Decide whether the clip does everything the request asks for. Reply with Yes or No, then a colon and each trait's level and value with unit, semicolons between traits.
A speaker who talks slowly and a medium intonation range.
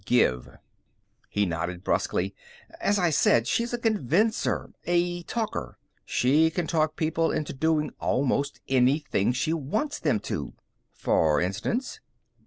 No: slow, 125 wpm; wide, 6.8 semitones